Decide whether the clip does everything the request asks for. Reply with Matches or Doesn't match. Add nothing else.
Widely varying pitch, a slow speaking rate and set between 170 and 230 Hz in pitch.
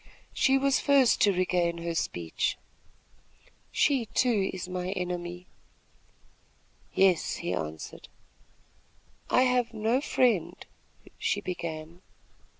Matches